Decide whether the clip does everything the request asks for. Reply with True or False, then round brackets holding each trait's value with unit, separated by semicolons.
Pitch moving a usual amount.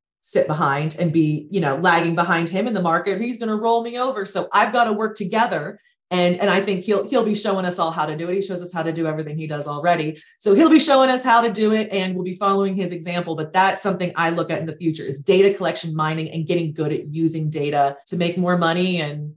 True (3.7 semitones)